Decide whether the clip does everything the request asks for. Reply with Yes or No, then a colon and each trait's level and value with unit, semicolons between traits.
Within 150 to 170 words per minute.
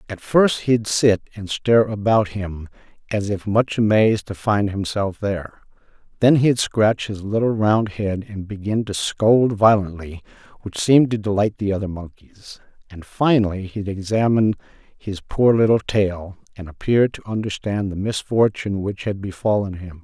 Yes: average, 160 wpm